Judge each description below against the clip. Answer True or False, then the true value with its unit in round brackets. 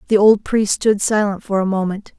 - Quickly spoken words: True (220 wpm)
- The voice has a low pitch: False (205 Hz)